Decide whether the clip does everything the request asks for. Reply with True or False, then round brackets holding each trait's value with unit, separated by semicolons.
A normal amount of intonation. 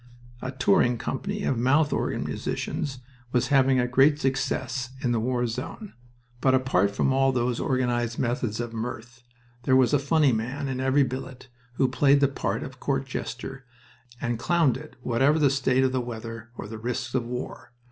False (2.0 semitones)